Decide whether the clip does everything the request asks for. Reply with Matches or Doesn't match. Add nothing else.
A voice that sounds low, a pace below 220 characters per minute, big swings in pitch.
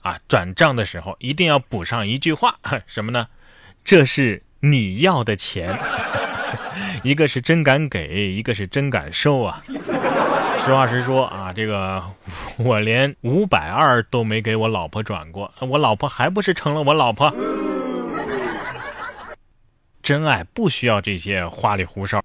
Matches